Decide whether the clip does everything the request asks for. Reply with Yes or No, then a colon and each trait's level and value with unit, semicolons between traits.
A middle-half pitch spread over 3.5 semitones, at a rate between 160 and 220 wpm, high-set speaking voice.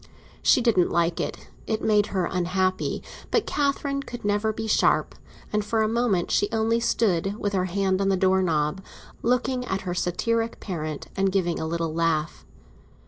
Yes: average, 4.1 semitones; average, 170 wpm; high, 195 Hz